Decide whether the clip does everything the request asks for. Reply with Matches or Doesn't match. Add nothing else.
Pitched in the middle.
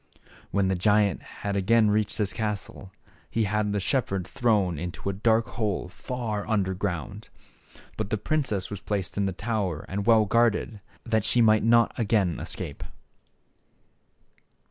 Doesn't match